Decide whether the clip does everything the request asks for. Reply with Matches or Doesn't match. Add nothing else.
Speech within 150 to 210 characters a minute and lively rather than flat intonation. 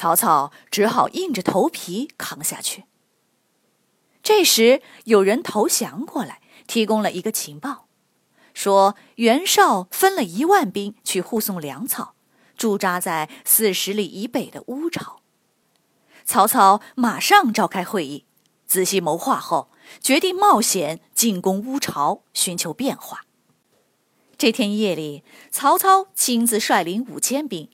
Matches